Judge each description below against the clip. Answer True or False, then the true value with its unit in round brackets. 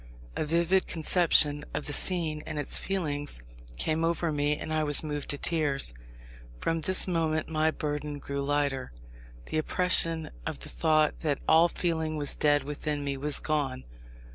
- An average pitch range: False (1.9 semitones)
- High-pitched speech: False (155 Hz)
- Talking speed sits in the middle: True (165 wpm)